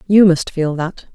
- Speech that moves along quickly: Yes, fast, 210 wpm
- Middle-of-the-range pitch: Yes, medium, 175 Hz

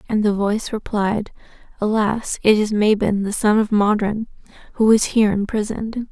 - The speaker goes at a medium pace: Yes, average, 155 wpm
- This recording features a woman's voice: Yes, female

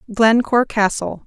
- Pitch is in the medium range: No, high, 220 Hz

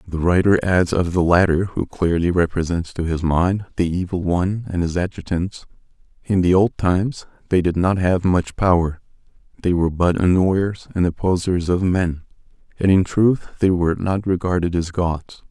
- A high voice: No, very low, 90 Hz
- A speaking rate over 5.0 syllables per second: No, 4.9 syllables/s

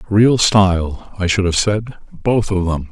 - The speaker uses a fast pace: No, average, 165 wpm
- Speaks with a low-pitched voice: Yes, low, 100 Hz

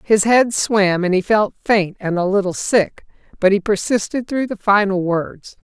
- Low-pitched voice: No, high, 200 Hz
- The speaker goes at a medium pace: Yes, average, 190 wpm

